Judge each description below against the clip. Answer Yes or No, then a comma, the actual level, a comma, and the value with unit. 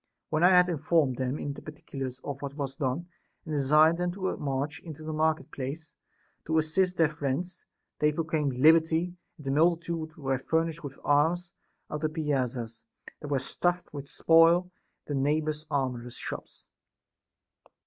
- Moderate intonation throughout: Yes, average, 3.1 semitones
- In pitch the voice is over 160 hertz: No, medium, 155 Hz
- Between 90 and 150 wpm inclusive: No, average, 165 wpm